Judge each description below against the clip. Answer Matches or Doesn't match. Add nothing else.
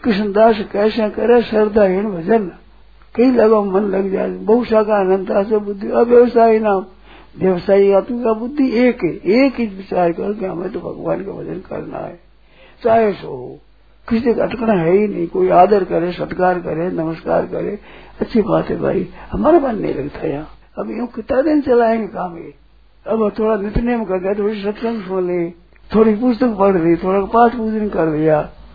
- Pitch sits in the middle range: Doesn't match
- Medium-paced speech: Matches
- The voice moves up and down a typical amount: Matches